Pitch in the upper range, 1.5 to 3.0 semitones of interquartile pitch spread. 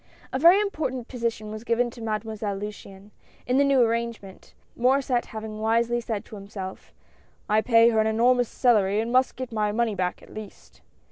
Yes: high, 230 Hz; narrow, 2.5 semitones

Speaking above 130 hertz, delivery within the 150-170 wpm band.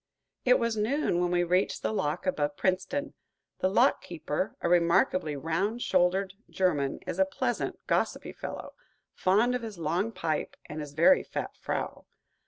Yes: medium, 185 Hz; average, 160 wpm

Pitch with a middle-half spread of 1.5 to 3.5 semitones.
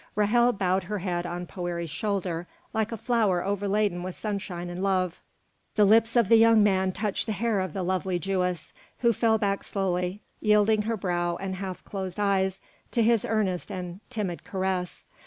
Yes: average, 2.8 semitones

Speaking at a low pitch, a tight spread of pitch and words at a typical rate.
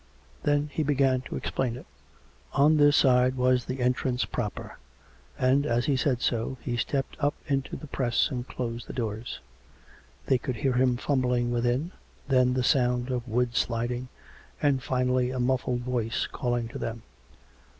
Yes: low, 125 Hz; narrow, 1.6 semitones; average, 160 wpm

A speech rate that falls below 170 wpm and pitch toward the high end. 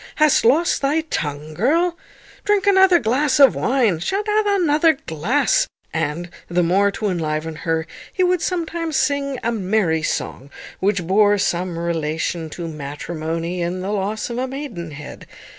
Yes: average, 150 wpm; high, 205 Hz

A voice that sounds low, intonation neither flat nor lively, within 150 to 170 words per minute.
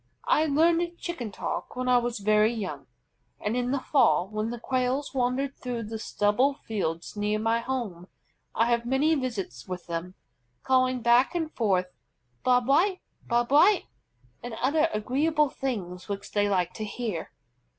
No: high, 240 Hz; average, 4.5 semitones; average, 160 wpm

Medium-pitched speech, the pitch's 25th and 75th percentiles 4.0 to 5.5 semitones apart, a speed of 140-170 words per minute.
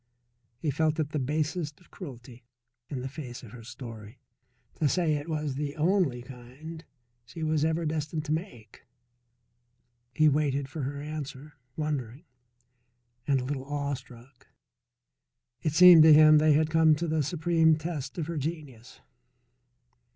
No: medium, 150 Hz; average, 3.0 semitones; average, 145 wpm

